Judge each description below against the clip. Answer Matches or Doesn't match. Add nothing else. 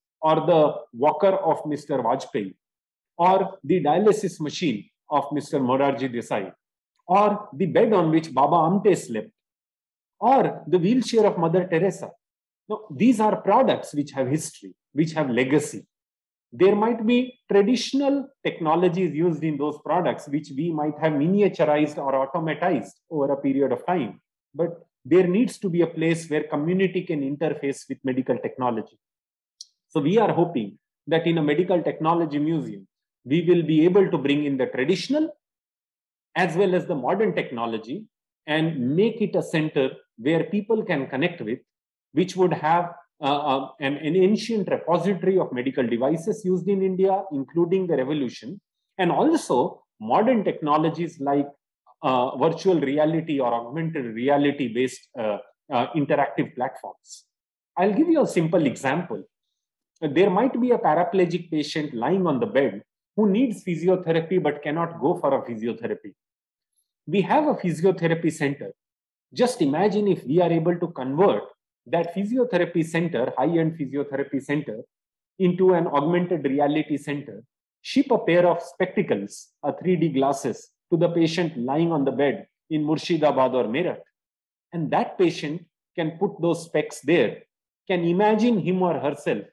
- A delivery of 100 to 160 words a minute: Matches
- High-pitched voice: Doesn't match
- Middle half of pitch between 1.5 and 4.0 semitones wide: Doesn't match